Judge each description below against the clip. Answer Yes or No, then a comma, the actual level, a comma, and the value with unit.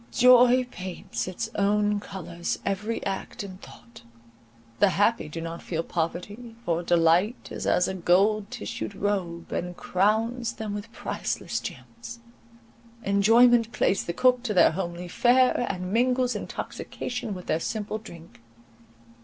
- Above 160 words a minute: No, slow, 135 wpm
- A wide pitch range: No, average, 4.6 semitones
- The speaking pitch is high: Yes, high, 205 Hz